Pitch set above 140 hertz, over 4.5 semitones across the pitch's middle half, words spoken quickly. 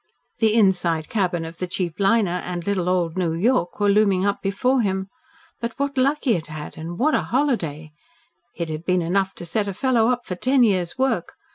Yes: high, 190 Hz; average, 5.0 semitones; fast, 210 wpm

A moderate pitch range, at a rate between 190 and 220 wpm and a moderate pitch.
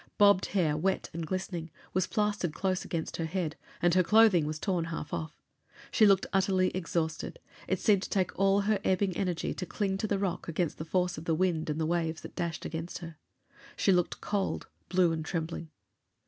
Yes: average, 3.0 semitones; average, 200 wpm; medium, 180 Hz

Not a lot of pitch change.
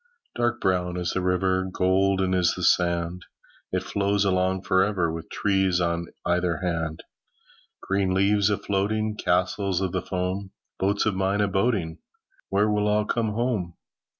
Yes: narrow, 2.1 semitones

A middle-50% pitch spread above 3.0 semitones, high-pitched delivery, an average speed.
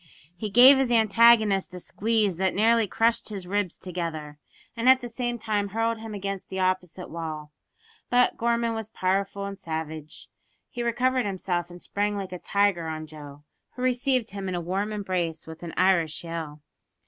Yes: average, 4.7 semitones; high, 195 Hz; average, 175 wpm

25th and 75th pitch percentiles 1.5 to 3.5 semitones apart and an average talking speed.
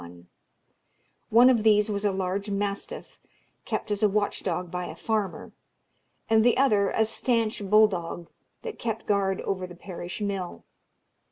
Yes: narrow, 2.5 semitones; average, 155 wpm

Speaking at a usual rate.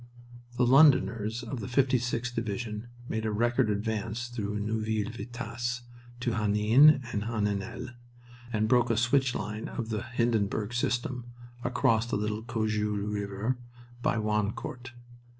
No: slow, 130 wpm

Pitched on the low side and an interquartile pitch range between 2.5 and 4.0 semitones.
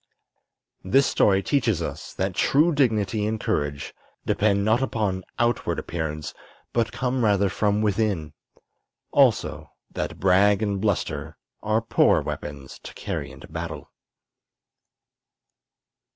Yes: low, 105 Hz; average, 3.2 semitones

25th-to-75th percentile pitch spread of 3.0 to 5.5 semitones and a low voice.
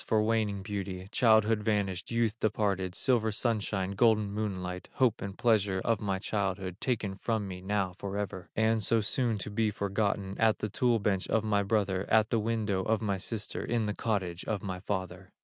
No: narrow, 2.5 semitones; low, 105 Hz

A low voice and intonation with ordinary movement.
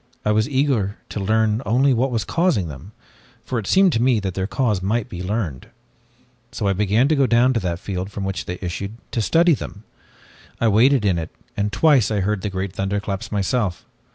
Yes: low, 105 Hz; average, 4.1 semitones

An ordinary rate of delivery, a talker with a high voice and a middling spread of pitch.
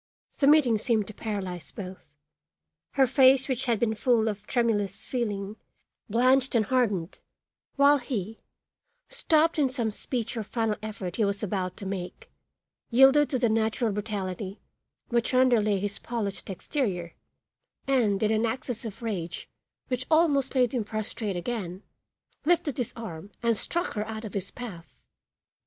Yes: average, 150 wpm; high, 225 Hz; average, 4.0 semitones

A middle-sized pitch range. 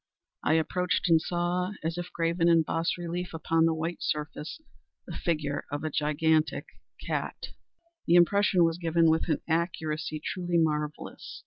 No: narrow, 1.7 semitones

